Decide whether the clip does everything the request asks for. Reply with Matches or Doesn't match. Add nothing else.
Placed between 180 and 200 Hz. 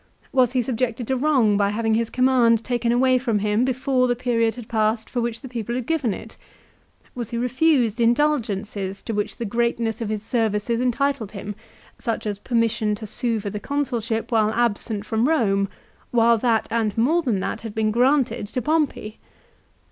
Doesn't match